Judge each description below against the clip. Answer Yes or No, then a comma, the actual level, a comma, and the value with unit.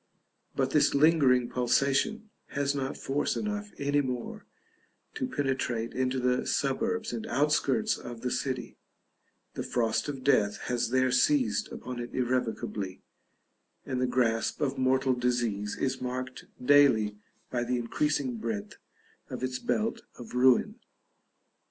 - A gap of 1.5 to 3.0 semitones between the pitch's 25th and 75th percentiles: Yes, average, 2.7 semitones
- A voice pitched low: Yes, low, 130 Hz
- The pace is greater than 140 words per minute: No, slow, 135 wpm